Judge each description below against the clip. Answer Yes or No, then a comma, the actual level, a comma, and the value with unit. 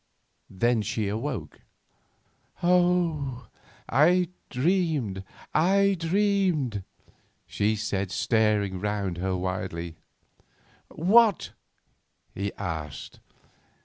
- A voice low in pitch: Yes, low, 115 Hz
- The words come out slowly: Yes, slow, 75 wpm